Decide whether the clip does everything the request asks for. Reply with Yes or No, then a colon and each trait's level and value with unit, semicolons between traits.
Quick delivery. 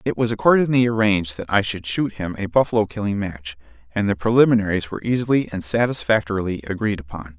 No: average, 180 wpm